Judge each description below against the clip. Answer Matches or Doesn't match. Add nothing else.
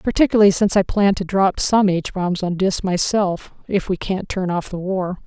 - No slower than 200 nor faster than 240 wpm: Matches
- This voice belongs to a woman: Matches